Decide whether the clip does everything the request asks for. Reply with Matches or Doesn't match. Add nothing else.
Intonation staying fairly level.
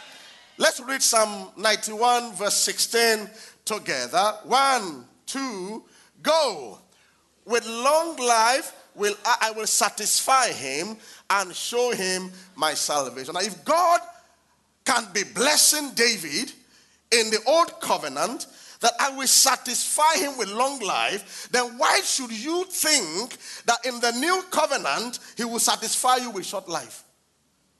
Doesn't match